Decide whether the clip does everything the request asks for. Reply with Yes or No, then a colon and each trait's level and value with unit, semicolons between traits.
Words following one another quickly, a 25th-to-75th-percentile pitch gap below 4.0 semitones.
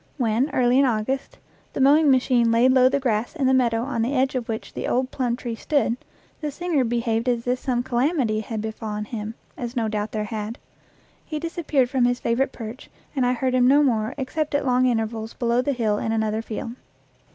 Yes: fast, 215 wpm; average, 2.7 semitones